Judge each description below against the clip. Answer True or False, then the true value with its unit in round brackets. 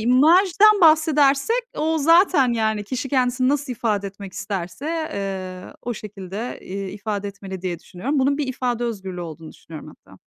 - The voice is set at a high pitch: True (235 Hz)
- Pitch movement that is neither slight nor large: False (6.4 semitones)